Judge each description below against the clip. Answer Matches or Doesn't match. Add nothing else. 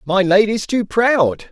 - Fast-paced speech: Doesn't match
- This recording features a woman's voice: Doesn't match